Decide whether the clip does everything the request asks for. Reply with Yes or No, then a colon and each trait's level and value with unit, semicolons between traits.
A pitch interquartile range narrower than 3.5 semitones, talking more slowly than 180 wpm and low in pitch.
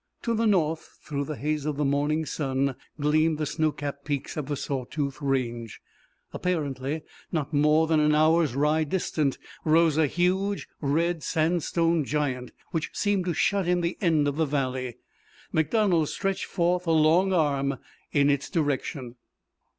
No: average, 3.0 semitones; average, 160 wpm; medium, 155 Hz